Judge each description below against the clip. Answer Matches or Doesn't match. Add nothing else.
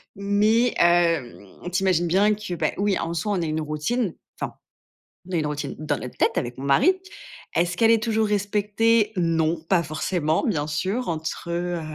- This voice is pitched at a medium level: Matches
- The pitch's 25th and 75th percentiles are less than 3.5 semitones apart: Doesn't match